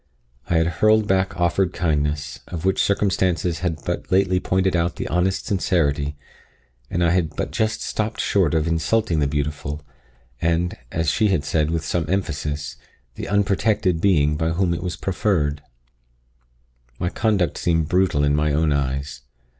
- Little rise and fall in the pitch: No, average, 3.9 semitones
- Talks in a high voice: No, very low, 85 Hz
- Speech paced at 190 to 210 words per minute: No, average, 160 wpm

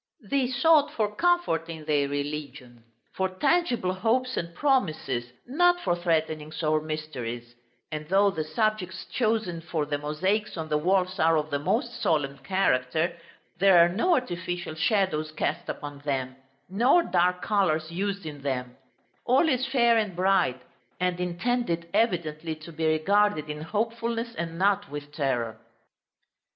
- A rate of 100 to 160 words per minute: Yes, average, 145 wpm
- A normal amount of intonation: No, wide, 5.8 semitones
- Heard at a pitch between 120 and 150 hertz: No, medium, 175 Hz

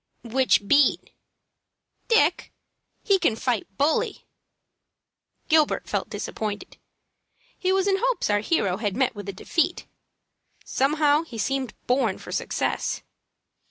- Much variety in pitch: Yes, wide, 7.0 semitones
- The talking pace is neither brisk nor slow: No, slow, 120 wpm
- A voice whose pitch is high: Yes, very high, 265 Hz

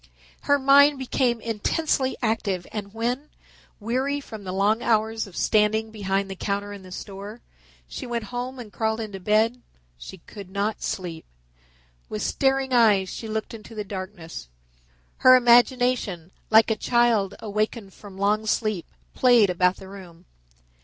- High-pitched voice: Yes, high, 215 Hz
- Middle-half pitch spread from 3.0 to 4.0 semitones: Yes, average, 3.5 semitones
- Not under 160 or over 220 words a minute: No, average, 150 wpm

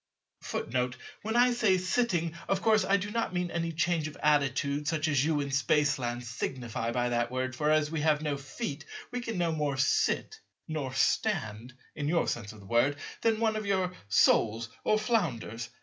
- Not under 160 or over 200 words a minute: Yes, average, 185 wpm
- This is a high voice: No, medium, 150 Hz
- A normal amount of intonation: No, wide, 6.2 semitones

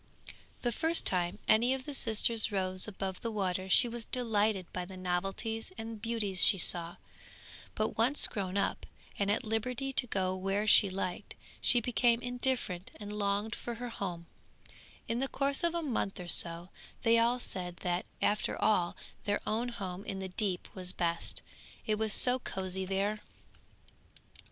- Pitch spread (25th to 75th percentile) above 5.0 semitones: No, average, 4.0 semitones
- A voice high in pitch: Yes, high, 210 Hz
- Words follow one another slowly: No, average, 165 wpm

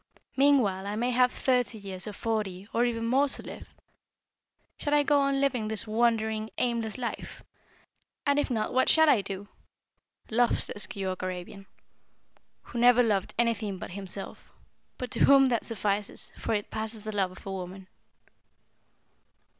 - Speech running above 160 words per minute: No, average, 155 wpm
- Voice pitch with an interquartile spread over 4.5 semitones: No, average, 3.8 semitones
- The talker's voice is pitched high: Yes, high, 220 Hz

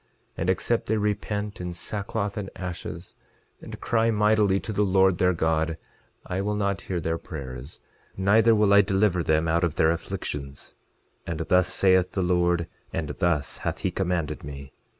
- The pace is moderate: Yes, average, 170 wpm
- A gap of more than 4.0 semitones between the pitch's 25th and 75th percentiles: No, average, 3.6 semitones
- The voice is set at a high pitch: No, very low, 90 Hz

